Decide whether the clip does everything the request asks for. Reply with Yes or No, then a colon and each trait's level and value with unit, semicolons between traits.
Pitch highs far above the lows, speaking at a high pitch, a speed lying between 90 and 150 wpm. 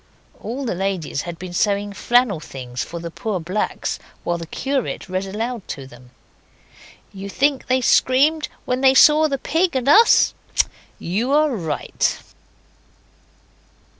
Yes: wide, 7.4 semitones; high, 210 Hz; average, 140 wpm